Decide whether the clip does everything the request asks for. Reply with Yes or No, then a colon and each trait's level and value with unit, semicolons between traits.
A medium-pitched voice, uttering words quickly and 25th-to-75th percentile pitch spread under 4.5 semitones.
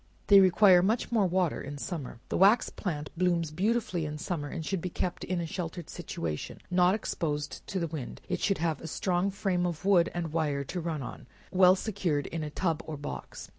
Yes: medium, 175 Hz; fast, 210 wpm; average, 3.4 semitones